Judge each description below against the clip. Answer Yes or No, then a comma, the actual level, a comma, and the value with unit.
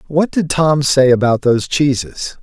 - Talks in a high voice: No, medium, 140 Hz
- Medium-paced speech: Yes, average, 175 wpm